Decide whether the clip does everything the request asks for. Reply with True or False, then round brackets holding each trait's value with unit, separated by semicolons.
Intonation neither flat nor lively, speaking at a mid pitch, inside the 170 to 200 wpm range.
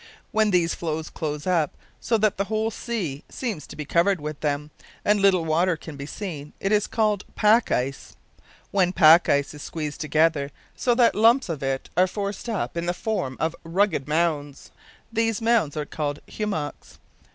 False (5.8 semitones; 170 Hz; 180 wpm)